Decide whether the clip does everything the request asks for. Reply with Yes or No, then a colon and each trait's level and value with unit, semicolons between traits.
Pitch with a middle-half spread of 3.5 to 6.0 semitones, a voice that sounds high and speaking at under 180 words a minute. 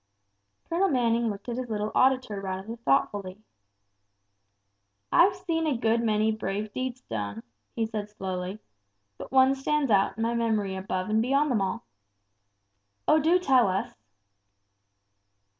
Yes: average, 4.7 semitones; high, 225 Hz; average, 140 wpm